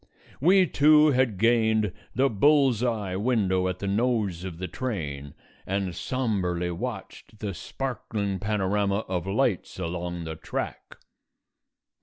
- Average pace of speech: No, slow, 125 wpm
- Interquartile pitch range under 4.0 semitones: No, average, 5.1 semitones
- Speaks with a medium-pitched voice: No, low, 100 Hz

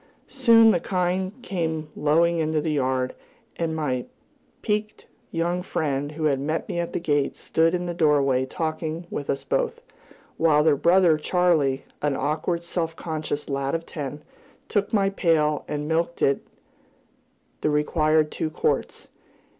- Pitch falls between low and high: Yes, medium, 160 Hz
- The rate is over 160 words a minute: No, average, 155 wpm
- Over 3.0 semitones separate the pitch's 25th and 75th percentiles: No, narrow, 2.6 semitones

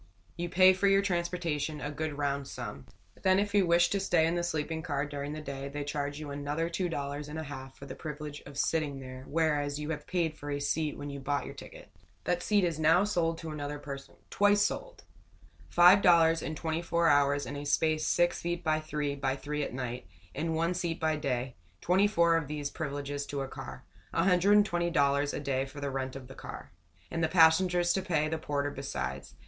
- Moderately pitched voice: Yes, medium, 155 Hz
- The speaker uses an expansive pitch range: No, average, 3.2 semitones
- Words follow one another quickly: Yes, fast, 215 wpm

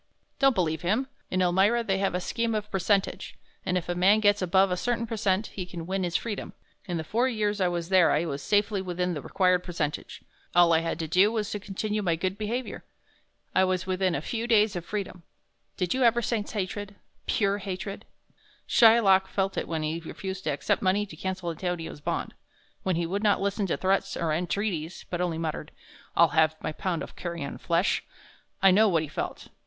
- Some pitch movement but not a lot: Yes, average, 3.1 semitones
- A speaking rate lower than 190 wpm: No, fast, 205 wpm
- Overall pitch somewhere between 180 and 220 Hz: Yes, high, 190 Hz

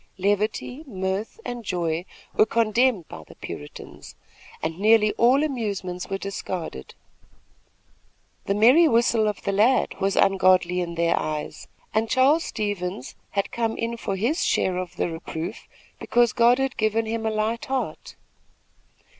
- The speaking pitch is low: No, high, 210 Hz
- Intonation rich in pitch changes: No, average, 4.2 semitones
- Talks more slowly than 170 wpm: Yes, average, 145 wpm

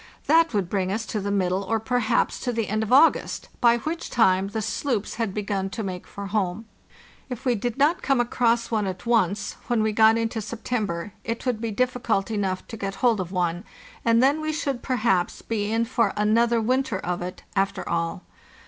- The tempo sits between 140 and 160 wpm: No, average, 200 wpm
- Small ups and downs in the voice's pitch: No, average, 3.5 semitones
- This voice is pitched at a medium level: No, high, 220 Hz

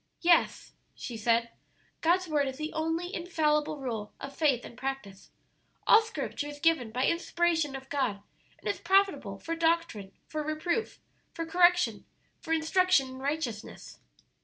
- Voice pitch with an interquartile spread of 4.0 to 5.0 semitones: Yes, average, 4.5 semitones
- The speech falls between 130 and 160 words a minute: Yes, average, 145 wpm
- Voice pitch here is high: Yes, very high, 305 Hz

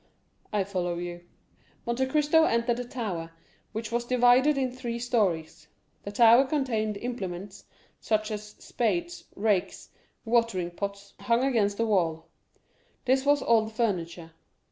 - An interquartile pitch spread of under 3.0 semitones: No, average, 4.0 semitones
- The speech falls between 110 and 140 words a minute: Yes, slow, 135 wpm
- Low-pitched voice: No, high, 225 Hz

